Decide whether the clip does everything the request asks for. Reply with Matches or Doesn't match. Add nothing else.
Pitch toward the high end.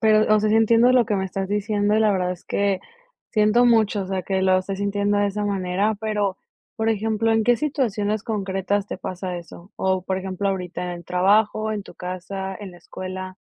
Matches